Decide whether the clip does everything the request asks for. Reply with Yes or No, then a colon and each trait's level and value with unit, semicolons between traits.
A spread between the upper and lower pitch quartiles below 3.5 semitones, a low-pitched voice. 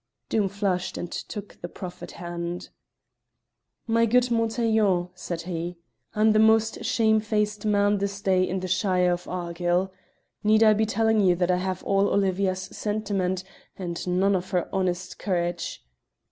No: average, 2.9 semitones; high, 190 Hz